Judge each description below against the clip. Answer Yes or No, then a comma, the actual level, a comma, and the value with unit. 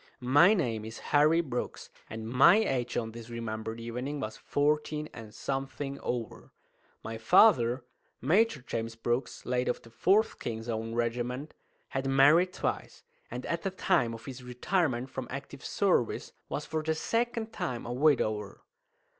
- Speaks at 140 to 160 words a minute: Yes, average, 155 wpm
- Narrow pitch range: No, average, 5.0 semitones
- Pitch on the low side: Yes, low, 125 Hz